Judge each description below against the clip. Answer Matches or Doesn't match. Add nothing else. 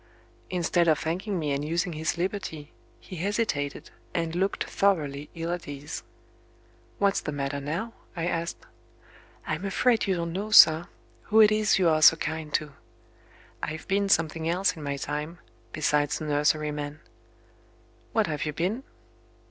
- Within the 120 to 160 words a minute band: Matches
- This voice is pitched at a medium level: Matches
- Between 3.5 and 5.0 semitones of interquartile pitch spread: Matches